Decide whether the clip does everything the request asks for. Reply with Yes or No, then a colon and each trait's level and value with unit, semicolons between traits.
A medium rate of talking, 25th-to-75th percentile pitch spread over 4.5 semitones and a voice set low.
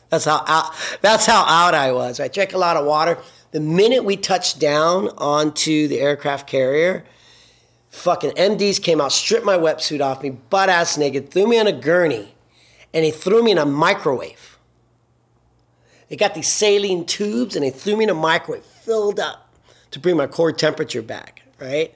No: average, 185 wpm; average, 5.2 semitones; medium, 170 Hz